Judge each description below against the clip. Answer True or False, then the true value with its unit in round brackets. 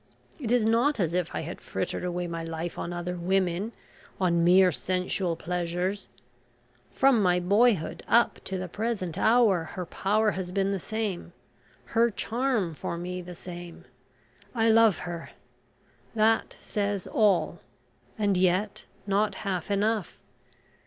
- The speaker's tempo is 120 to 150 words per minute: True (140 wpm)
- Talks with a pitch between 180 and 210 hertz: True (190 Hz)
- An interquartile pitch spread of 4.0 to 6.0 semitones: False (3.6 semitones)